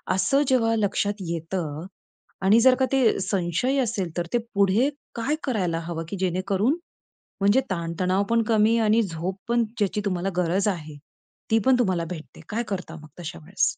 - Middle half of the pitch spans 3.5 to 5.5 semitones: Yes, average, 4.7 semitones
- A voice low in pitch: No, high, 195 Hz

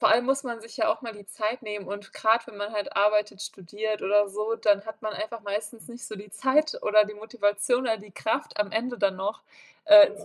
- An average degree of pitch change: No, narrow, 1.9 semitones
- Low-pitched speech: No, high, 215 Hz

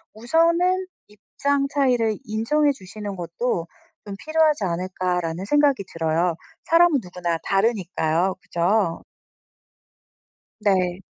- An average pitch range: No, wide, 8.0 semitones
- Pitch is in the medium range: No, high, 205 Hz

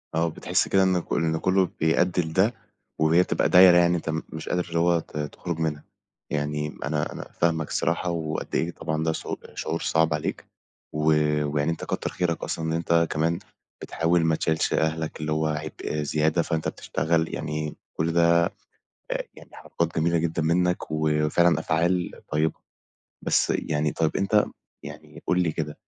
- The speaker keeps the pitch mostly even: Yes, narrow, 1.6 semitones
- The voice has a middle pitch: No, very low, 80 Hz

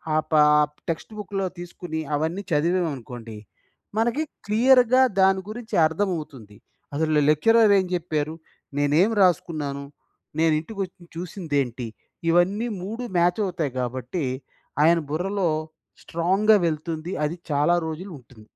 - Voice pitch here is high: No, medium, 165 Hz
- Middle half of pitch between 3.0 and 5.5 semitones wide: Yes, average, 4.3 semitones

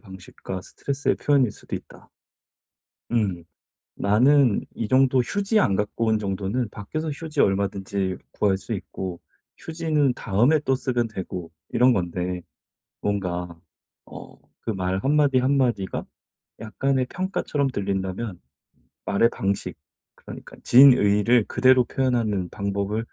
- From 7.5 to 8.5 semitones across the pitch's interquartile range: No, wide, 5.4 semitones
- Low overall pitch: Yes, low, 110 Hz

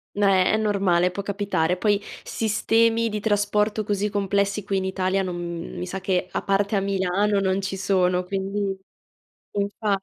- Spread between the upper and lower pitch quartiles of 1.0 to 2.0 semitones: Yes, narrow, 1.5 semitones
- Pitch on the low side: No, high, 195 Hz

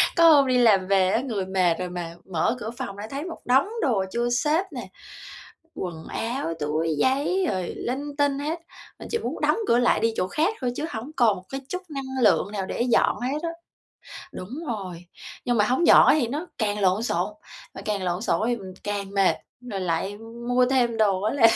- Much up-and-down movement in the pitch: Yes, wide, 5.8 semitones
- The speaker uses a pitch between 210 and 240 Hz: Yes, high, 230 Hz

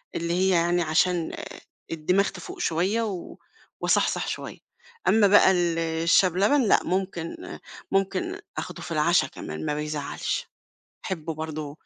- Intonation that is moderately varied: Yes, average, 3.2 semitones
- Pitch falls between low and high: Yes, medium, 175 Hz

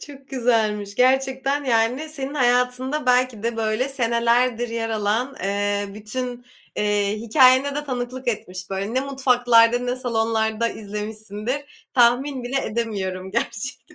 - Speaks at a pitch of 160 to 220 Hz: No, high, 240 Hz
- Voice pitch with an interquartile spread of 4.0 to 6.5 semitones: No, average, 3.1 semitones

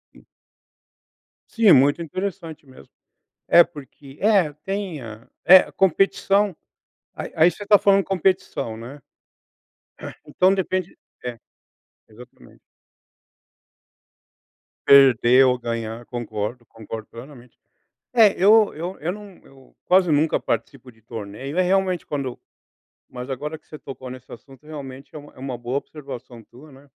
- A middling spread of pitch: No, wide, 6.9 semitones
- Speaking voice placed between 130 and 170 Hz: Yes, medium, 140 Hz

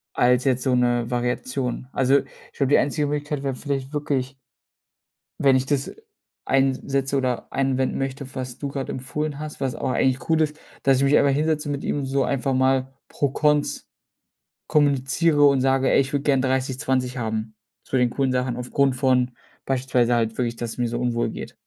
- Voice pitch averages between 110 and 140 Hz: Yes, low, 135 Hz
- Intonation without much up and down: Yes, narrow, 1.8 semitones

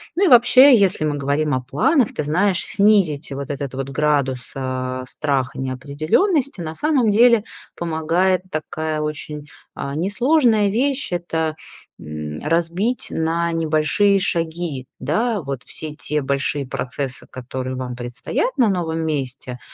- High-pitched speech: No, medium, 155 Hz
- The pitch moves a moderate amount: No, wide, 6.5 semitones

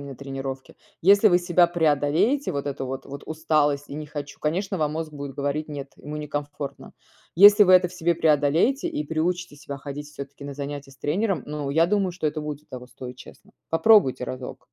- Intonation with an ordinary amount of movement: Yes, average, 3.6 semitones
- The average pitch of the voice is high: No, medium, 150 Hz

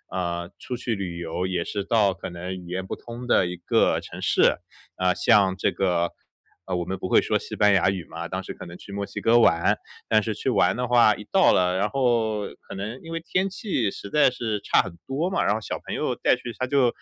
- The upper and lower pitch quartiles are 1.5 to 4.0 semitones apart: No, average, 4.7 semitones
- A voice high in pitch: No, low, 100 Hz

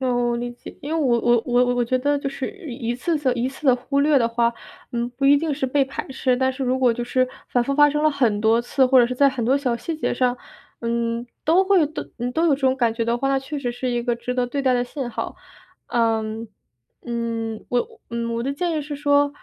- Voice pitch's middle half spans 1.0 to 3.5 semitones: Yes, average, 2.9 semitones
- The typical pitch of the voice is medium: No, very high, 255 Hz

